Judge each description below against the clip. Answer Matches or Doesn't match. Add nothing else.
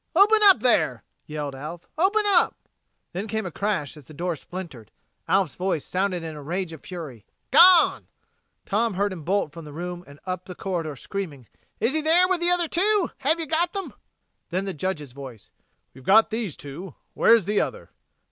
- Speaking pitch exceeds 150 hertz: Matches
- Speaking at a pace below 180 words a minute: Doesn't match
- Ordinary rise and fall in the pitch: Doesn't match